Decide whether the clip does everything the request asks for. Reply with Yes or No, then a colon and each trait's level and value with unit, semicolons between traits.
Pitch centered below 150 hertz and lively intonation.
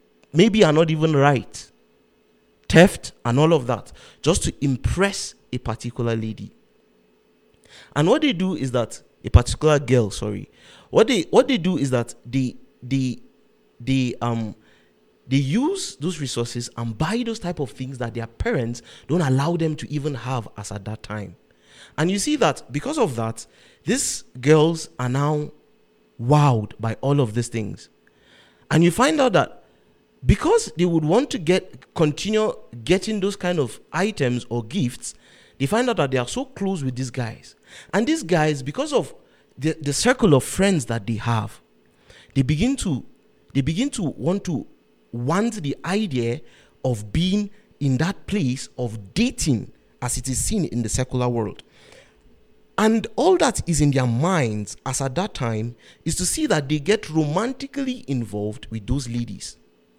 Yes: low, 135 Hz; wide, 7.1 semitones